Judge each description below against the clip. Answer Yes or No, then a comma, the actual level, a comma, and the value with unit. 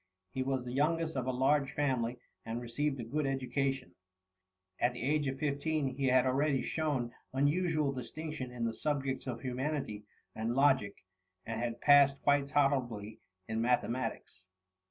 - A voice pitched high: No, low, 135 Hz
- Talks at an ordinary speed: Yes, average, 155 wpm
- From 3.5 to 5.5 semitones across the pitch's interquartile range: No, average, 3.0 semitones